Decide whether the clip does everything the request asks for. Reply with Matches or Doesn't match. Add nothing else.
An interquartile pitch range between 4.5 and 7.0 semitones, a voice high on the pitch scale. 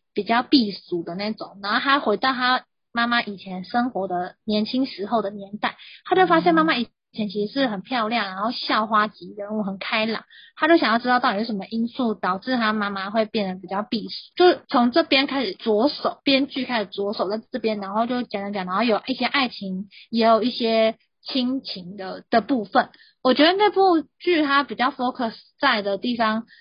Doesn't match